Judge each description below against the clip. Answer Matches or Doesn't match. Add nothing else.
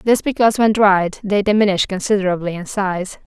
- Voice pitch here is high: Matches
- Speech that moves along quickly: Doesn't match